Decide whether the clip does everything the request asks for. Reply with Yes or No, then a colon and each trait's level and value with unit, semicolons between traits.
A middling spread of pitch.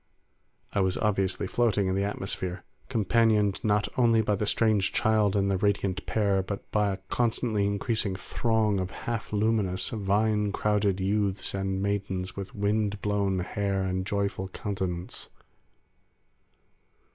No: narrow, 1.8 semitones